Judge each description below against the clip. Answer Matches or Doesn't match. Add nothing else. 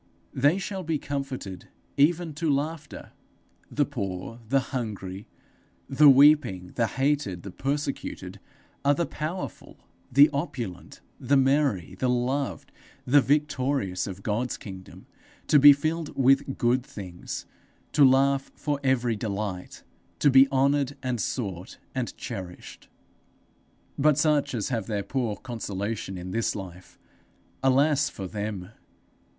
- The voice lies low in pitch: Matches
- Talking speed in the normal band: Doesn't match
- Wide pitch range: Matches